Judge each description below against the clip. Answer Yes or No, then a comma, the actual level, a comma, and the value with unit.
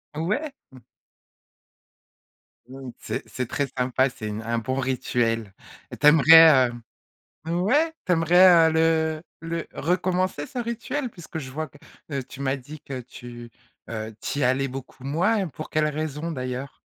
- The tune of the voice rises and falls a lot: No, average, 4.6 semitones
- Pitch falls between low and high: Yes, medium, 150 Hz